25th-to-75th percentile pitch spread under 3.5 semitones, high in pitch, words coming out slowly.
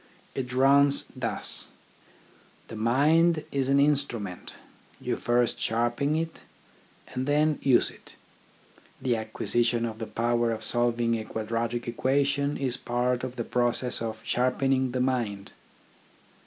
No: average, 2.9 semitones; low, 125 Hz; slow, 130 wpm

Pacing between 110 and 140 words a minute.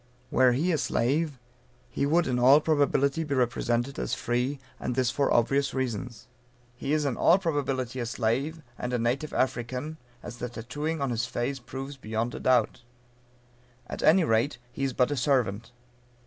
No: average, 175 wpm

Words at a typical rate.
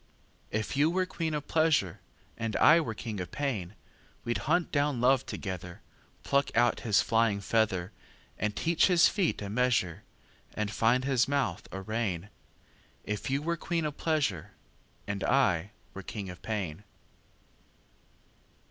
No: slow, 125 wpm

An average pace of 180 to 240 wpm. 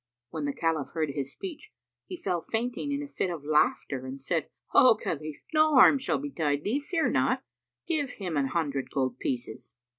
Yes: average, 185 wpm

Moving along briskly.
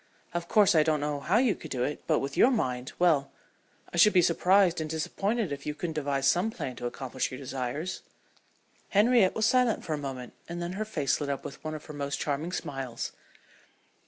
Yes: fast, 215 wpm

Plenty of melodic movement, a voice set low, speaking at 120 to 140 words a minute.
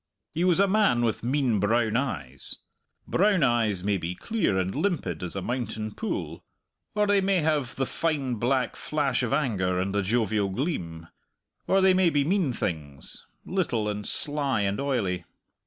No: wide, 7.7 semitones; low, 120 Hz; average, 170 wpm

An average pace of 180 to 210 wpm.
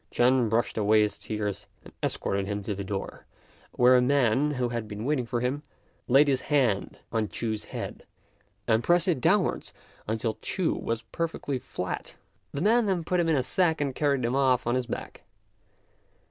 Yes: average, 185 wpm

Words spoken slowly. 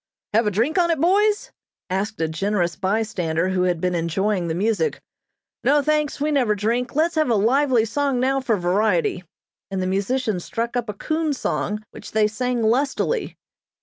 No: average, 180 wpm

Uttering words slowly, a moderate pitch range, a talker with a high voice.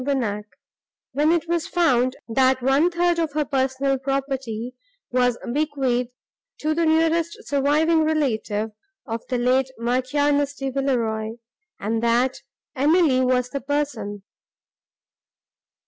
Yes: slow, 115 wpm; average, 3.3 semitones; very high, 270 Hz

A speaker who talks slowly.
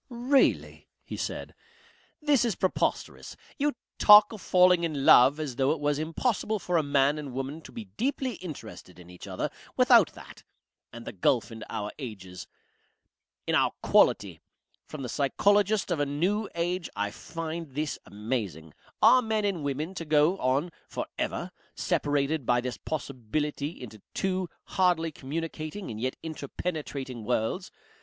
No: average, 155 wpm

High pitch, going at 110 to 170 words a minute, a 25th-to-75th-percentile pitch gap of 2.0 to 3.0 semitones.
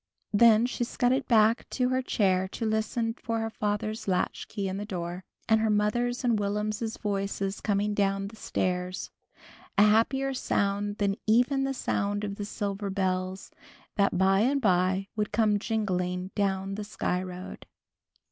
Yes: high, 205 Hz; average, 155 wpm; narrow, 2.4 semitones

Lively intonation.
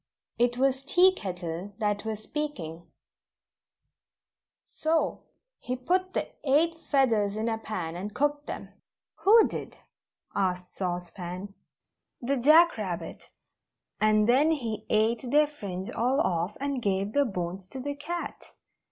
Yes: wide, 7.1 semitones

